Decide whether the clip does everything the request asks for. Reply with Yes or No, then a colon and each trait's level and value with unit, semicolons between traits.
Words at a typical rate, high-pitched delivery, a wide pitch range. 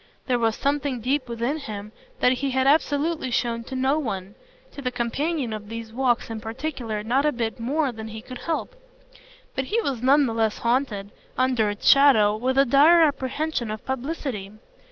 No: average, 185 wpm; very high, 255 Hz; average, 3.9 semitones